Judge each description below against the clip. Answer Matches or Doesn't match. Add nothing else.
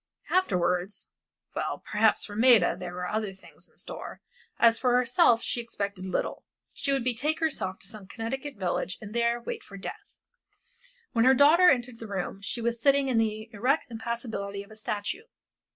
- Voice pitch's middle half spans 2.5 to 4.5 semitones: Matches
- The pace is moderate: Matches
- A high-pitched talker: Matches